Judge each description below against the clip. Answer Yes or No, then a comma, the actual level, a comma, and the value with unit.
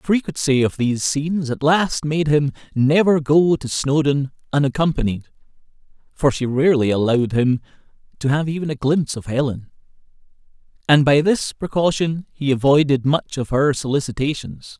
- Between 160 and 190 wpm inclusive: No, average, 145 wpm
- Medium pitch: Yes, medium, 145 Hz